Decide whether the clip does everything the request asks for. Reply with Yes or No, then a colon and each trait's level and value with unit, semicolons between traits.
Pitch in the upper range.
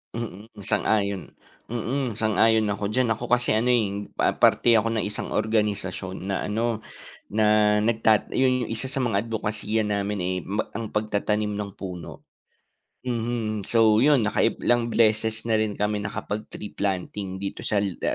No: low, 110 Hz